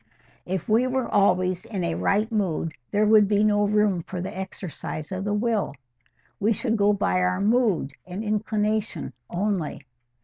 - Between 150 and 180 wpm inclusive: Yes, average, 165 wpm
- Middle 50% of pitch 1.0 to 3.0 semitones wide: Yes, average, 2.7 semitones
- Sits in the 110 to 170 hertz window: No, high, 205 Hz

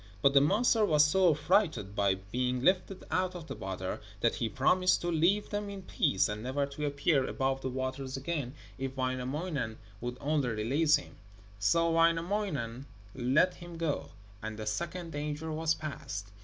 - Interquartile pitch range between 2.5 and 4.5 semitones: No, average, 5.1 semitones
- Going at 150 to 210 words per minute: Yes, average, 170 wpm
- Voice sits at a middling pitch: Yes, medium, 145 Hz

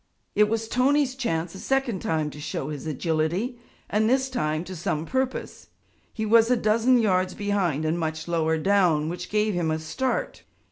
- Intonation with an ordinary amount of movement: No, wide, 6.5 semitones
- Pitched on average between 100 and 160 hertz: No, high, 190 Hz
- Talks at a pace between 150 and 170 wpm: No, average, 180 wpm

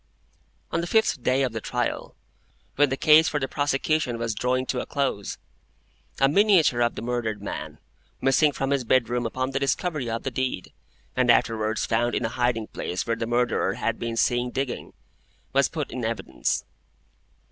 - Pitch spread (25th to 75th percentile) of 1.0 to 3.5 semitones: Yes, average, 3.0 semitones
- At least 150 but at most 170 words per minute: No, average, 180 wpm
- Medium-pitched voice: No, low, 125 Hz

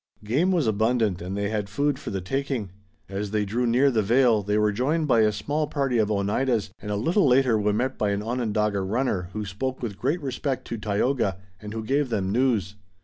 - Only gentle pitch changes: No, average, 4.3 semitones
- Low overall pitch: Yes, low, 110 Hz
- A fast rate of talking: Yes, fast, 215 wpm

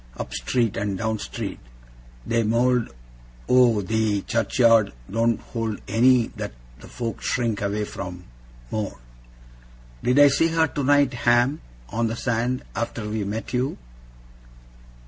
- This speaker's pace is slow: Yes, slow, 130 wpm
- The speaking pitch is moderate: No, low, 115 Hz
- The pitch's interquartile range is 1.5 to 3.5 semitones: Yes, narrow, 2.5 semitones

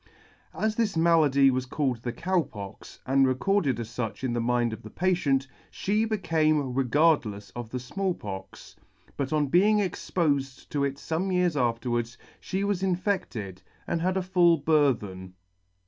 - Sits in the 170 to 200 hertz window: No, medium, 140 Hz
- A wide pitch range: Yes, wide, 6.8 semitones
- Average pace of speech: Yes, average, 160 wpm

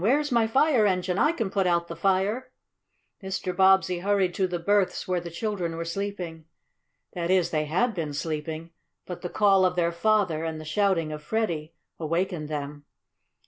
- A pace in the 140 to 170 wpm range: No, average, 180 wpm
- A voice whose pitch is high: No, medium, 180 Hz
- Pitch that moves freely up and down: No, average, 3.4 semitones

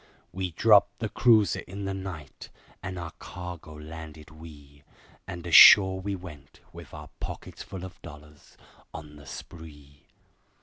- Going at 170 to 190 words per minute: No, average, 140 wpm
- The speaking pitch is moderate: No, very low, 85 Hz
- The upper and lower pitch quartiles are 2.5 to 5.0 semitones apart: Yes, average, 4.0 semitones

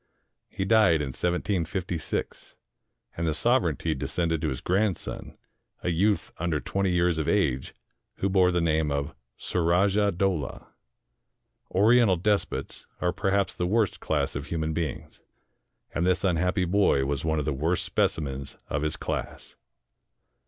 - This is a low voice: Yes, very low, 85 Hz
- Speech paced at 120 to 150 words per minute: Yes, average, 145 wpm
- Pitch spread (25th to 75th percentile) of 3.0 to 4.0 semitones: Yes, average, 3.7 semitones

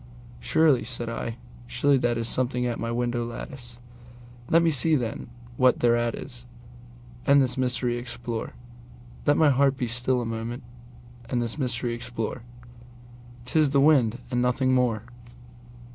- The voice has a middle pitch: No, low, 120 Hz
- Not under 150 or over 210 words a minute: No, average, 140 wpm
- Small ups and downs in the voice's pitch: Yes, narrow, 1.4 semitones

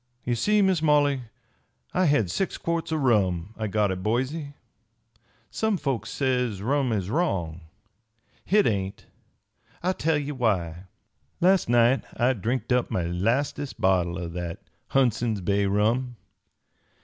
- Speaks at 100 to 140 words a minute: Yes, slow, 135 wpm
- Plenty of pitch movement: Yes, wide, 6.7 semitones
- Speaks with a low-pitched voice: Yes, low, 120 Hz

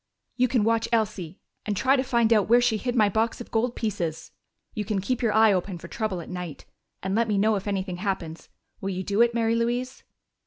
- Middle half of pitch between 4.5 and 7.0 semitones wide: No, average, 3.5 semitones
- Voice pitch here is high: Yes, high, 215 Hz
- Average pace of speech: No, fast, 230 wpm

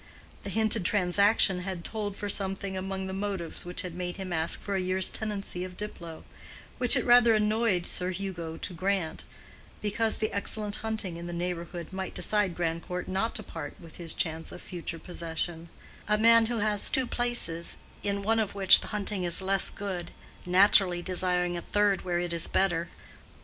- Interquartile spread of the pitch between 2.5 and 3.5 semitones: Yes, average, 3.0 semitones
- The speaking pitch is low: No, high, 190 Hz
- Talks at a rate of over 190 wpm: No, average, 180 wpm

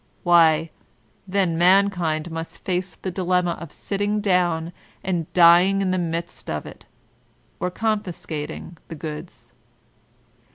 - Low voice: No, medium, 175 Hz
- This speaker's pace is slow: Yes, slow, 125 wpm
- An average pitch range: No, narrow, 2.3 semitones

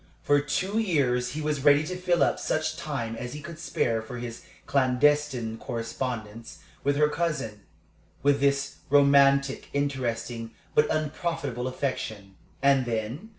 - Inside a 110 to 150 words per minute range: Yes, average, 140 wpm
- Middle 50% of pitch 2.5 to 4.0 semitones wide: Yes, average, 3.6 semitones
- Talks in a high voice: No, medium, 140 Hz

